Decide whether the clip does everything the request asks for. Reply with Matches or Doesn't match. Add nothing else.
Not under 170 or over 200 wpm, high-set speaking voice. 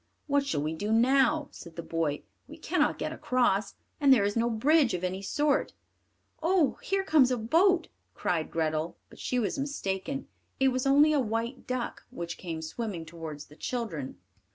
Matches